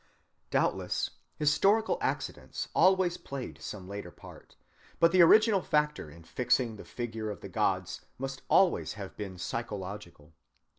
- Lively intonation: Yes, wide, 8.8 semitones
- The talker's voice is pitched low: Yes, low, 120 Hz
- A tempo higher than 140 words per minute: No, slow, 135 wpm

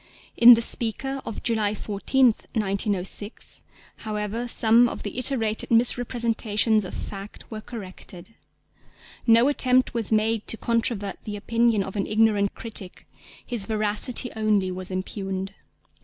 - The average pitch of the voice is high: Yes, high, 220 Hz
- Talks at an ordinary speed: No, slow, 125 wpm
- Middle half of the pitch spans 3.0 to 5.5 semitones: No, narrow, 2.4 semitones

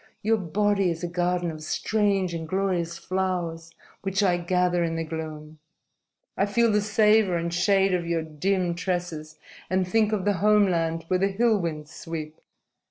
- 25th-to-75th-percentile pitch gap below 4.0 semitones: Yes, average, 3.1 semitones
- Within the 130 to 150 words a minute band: No, average, 170 wpm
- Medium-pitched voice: Yes, medium, 180 Hz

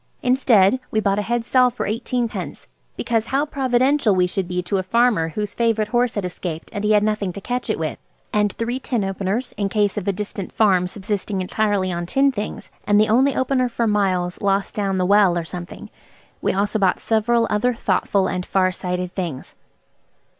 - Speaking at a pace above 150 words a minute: Yes, average, 195 wpm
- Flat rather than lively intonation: No, average, 3.8 semitones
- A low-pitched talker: No, high, 210 Hz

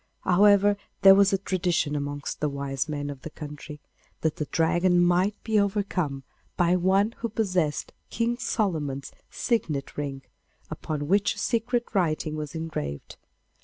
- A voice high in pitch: No, medium, 175 Hz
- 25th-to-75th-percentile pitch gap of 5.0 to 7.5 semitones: Yes, wide, 5.4 semitones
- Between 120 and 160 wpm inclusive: Yes, average, 145 wpm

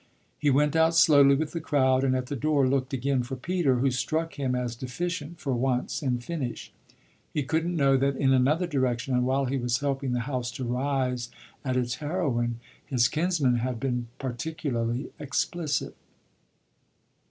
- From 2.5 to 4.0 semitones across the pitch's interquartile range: Yes, average, 3.0 semitones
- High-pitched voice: No, low, 135 Hz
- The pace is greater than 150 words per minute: Yes, average, 170 wpm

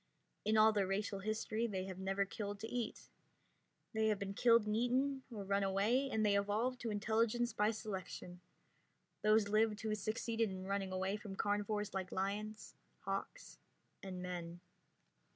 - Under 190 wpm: Yes, average, 160 wpm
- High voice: Yes, high, 210 Hz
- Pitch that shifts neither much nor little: No, narrow, 2.2 semitones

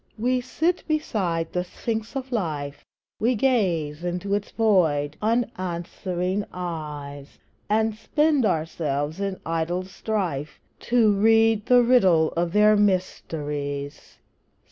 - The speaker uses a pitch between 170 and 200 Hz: Yes, medium, 185 Hz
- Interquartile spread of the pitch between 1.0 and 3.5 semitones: No, wide, 5.6 semitones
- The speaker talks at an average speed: No, slow, 110 wpm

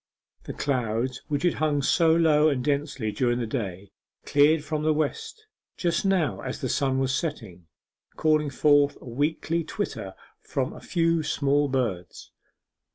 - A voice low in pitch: No, medium, 145 Hz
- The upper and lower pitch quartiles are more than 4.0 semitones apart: No, average, 3.6 semitones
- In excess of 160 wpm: No, average, 155 wpm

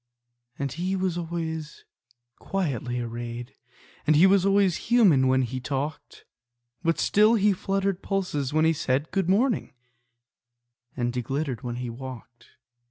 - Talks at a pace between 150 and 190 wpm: No, average, 140 wpm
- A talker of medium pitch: Yes, medium, 155 Hz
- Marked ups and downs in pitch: Yes, wide, 6.9 semitones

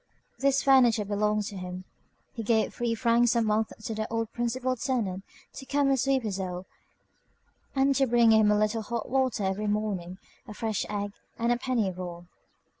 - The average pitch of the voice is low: No, high, 220 Hz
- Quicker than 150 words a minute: Yes, average, 185 wpm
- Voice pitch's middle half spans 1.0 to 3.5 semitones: Yes, average, 2.9 semitones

